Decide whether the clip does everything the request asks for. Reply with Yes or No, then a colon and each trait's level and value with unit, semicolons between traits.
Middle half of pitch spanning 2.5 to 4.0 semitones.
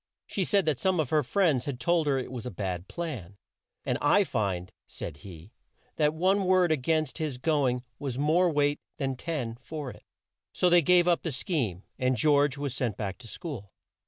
No: average, 5.2 semitones